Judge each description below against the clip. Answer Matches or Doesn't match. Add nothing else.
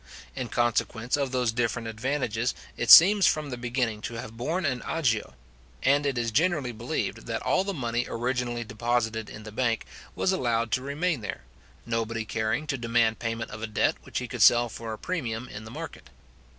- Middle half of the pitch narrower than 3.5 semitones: Matches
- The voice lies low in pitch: Matches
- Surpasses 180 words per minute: Matches